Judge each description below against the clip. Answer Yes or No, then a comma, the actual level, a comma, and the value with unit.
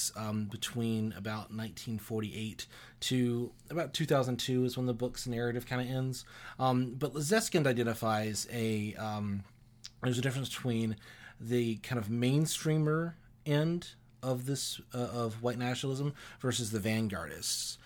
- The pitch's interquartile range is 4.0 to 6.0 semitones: No, average, 2.7 semitones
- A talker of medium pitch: No, low, 120 Hz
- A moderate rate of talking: No, slow, 130 wpm